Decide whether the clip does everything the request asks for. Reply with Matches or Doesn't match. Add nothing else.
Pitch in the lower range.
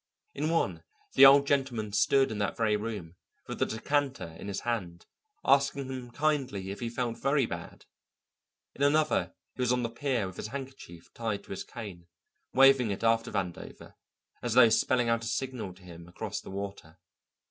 Matches